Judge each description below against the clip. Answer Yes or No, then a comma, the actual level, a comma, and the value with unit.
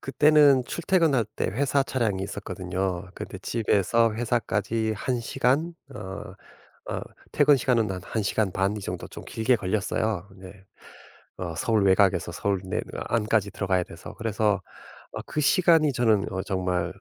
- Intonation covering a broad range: No, average, 4.3 semitones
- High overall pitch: No, low, 105 Hz